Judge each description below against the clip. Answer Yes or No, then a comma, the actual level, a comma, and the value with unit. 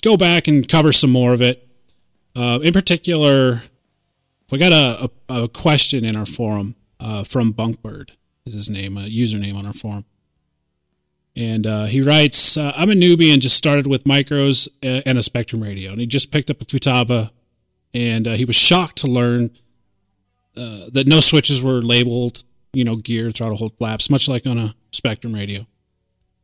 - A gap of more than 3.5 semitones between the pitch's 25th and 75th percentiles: Yes, average, 4.1 semitones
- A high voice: No, low, 120 Hz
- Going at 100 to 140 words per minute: No, average, 185 wpm